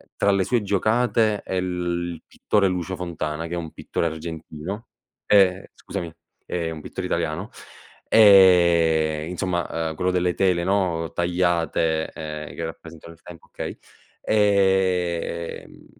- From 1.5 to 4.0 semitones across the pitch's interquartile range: Yes, narrow, 2.6 semitones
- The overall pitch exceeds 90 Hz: No, very low, 85 Hz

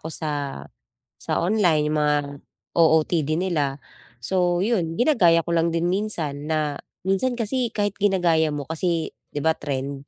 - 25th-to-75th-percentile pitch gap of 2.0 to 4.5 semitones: Yes, average, 4.1 semitones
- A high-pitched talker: No, medium, 165 Hz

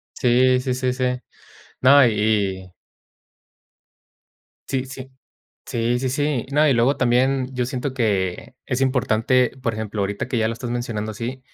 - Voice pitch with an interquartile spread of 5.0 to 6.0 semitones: No, average, 2.7 semitones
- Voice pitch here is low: Yes, low, 125 Hz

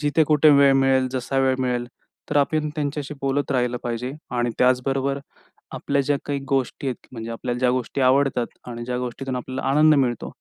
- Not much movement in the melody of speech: Yes, narrow, 2.2 semitones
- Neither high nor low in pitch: No, low, 130 Hz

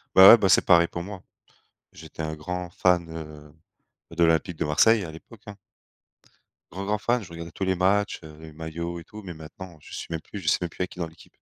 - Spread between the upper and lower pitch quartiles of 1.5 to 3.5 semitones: Yes, average, 2.9 semitones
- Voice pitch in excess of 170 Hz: No, very low, 85 Hz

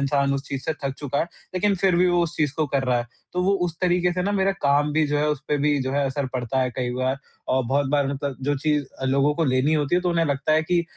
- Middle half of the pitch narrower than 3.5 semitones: No, average, 3.8 semitones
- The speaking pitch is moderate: Yes, medium, 145 Hz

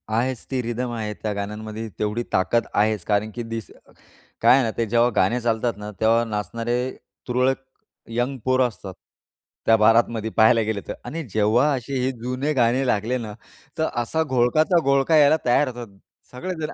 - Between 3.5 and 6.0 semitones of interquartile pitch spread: No, average, 2.8 semitones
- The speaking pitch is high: No, low, 120 Hz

